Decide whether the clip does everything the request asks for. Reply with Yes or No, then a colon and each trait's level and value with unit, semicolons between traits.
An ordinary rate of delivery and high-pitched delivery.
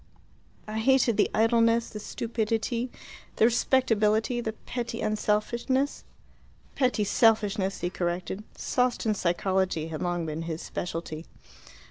No: slow, 110 wpm; high, 215 Hz